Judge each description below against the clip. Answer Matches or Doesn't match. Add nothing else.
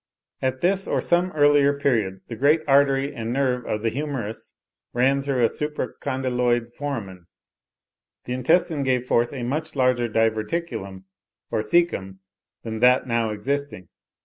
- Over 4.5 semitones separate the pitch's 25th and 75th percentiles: Doesn't match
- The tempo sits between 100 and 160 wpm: Matches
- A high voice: Doesn't match